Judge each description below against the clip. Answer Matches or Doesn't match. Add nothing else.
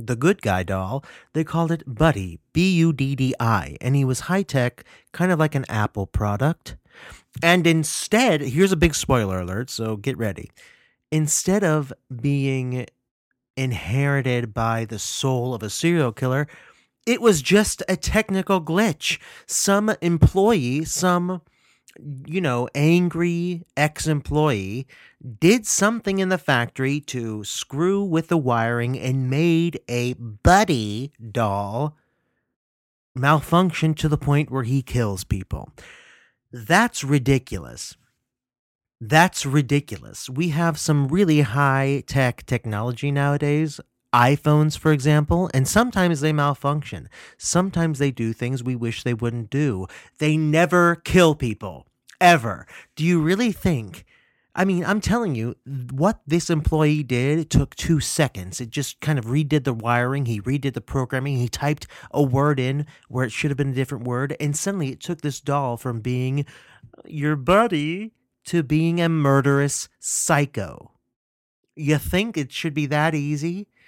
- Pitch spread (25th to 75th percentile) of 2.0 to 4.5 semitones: Doesn't match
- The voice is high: Doesn't match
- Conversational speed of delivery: Matches